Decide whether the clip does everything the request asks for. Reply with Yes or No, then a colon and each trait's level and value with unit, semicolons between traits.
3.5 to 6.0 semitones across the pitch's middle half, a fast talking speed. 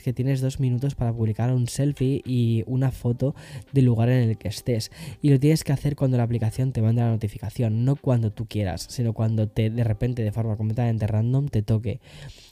No: average, 3.0 semitones; fast, 210 wpm